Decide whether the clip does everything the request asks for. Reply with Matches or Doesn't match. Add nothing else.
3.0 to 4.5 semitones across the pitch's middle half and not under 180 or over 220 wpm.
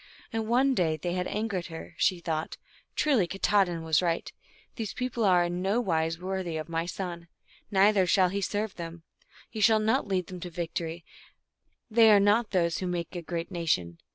Matches